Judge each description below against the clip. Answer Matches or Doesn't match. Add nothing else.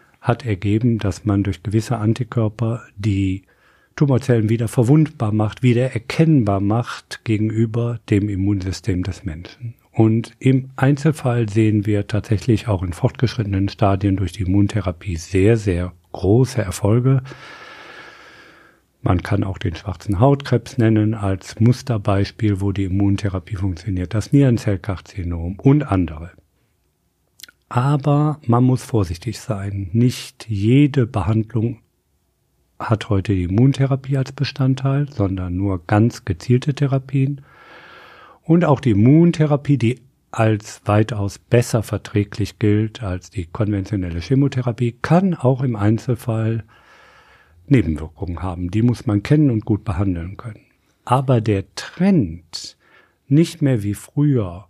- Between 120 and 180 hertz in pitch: Doesn't match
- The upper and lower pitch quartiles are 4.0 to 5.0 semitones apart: Matches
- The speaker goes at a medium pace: Doesn't match